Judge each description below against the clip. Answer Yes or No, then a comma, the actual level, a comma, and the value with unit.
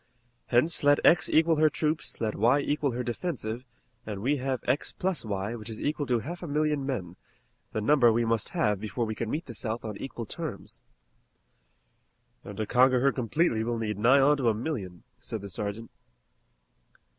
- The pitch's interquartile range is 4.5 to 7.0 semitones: Yes, average, 4.9 semitones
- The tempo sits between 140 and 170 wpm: No, average, 190 wpm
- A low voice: Yes, low, 120 Hz